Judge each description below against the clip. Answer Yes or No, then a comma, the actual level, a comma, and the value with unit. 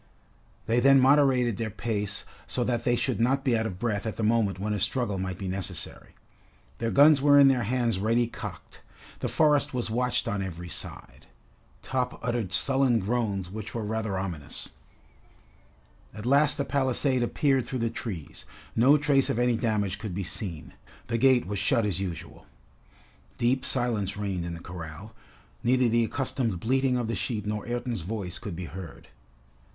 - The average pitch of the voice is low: Yes, low, 115 Hz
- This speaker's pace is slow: No, average, 175 wpm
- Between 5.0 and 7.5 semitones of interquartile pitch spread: No, average, 4.2 semitones